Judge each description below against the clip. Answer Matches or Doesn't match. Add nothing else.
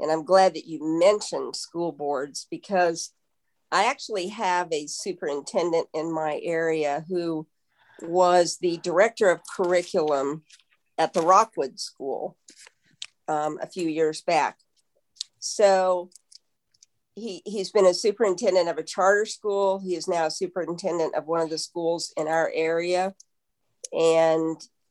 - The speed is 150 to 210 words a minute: Doesn't match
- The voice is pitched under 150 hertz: Doesn't match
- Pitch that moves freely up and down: Doesn't match